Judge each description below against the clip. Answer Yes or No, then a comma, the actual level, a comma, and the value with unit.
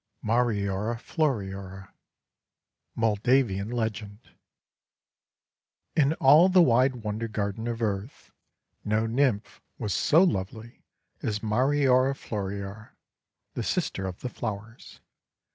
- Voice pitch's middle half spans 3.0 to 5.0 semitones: Yes, average, 3.9 semitones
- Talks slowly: Yes, slow, 95 wpm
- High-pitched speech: No, low, 110 Hz